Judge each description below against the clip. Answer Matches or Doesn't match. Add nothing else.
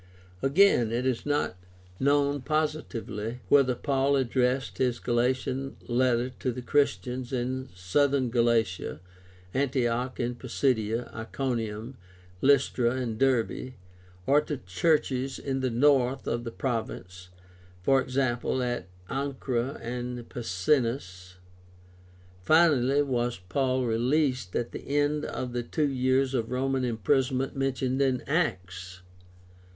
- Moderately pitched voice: Doesn't match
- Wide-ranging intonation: Doesn't match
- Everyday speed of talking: Doesn't match